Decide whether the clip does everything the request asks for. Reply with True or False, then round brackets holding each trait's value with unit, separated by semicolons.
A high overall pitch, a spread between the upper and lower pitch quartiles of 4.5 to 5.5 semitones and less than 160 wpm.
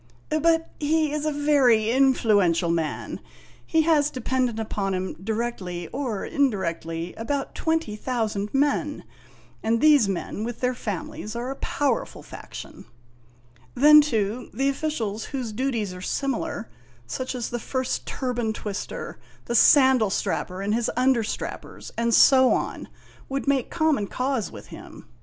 True (240 Hz; 4.8 semitones; 140 wpm)